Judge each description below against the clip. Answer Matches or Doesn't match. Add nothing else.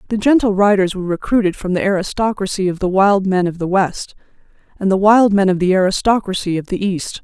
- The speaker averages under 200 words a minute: Doesn't match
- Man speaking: Doesn't match